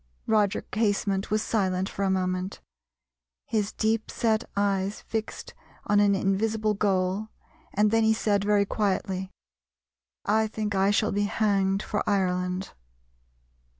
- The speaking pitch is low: No, high, 205 Hz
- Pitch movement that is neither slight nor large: No, narrow, 2.0 semitones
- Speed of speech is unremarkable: No, slow, 125 wpm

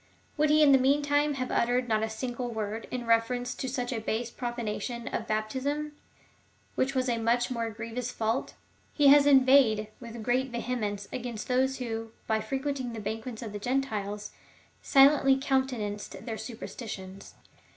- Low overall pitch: No, high, 245 Hz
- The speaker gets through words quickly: No, average, 160 wpm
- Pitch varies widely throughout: No, average, 3.1 semitones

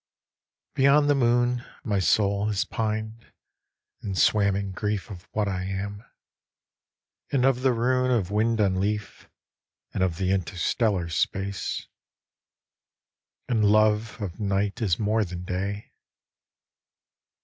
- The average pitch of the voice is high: No, low, 105 Hz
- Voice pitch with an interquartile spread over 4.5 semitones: No, average, 2.8 semitones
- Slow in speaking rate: Yes, slow, 125 wpm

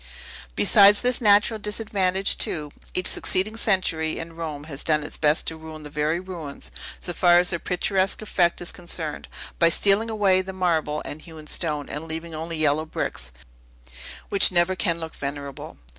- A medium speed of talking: Yes, average, 170 wpm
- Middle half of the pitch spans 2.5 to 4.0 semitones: Yes, average, 3.4 semitones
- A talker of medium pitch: Yes, medium, 170 Hz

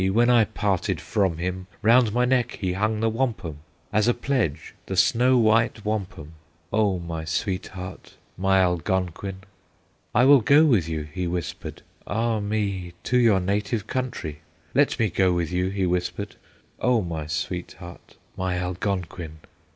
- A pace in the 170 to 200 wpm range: No, average, 150 wpm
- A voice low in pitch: Yes, very low, 95 Hz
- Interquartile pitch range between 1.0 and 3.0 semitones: No, average, 4.1 semitones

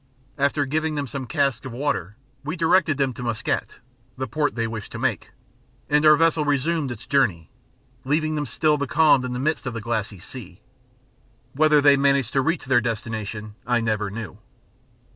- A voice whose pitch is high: No, low, 135 Hz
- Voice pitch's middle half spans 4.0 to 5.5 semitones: Yes, average, 4.6 semitones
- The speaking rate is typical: Yes, average, 180 wpm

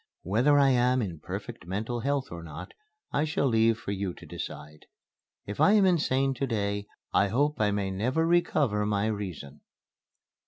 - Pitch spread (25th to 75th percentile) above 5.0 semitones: Yes, wide, 5.4 semitones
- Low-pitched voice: Yes, low, 110 Hz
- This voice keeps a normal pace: Yes, average, 170 wpm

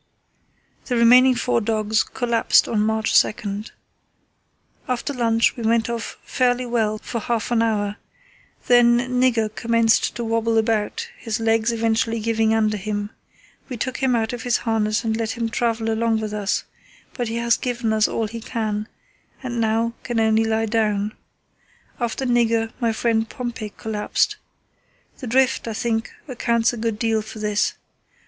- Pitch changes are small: Yes, narrow, 1.4 semitones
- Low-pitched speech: No, high, 225 Hz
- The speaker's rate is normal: Yes, average, 160 wpm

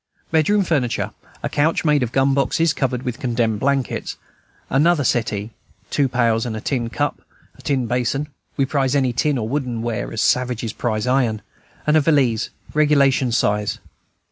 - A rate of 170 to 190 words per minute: No, average, 155 wpm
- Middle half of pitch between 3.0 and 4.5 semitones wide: Yes, average, 3.5 semitones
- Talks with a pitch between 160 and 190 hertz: No, low, 130 Hz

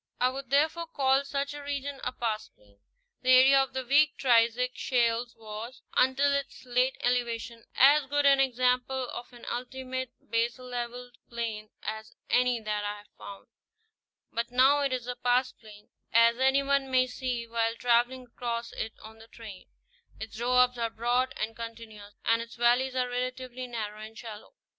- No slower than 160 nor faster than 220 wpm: Yes, average, 165 wpm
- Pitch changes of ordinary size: No, narrow, 2.2 semitones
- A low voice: No, high, 245 Hz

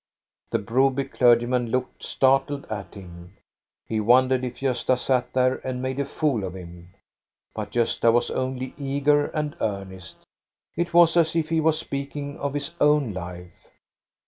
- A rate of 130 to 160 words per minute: Yes, average, 155 wpm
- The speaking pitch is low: Yes, low, 130 Hz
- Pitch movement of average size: Yes, average, 4.6 semitones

